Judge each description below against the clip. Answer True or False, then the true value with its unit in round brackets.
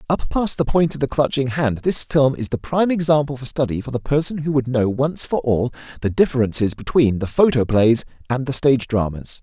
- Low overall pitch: True (130 Hz)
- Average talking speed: False (215 wpm)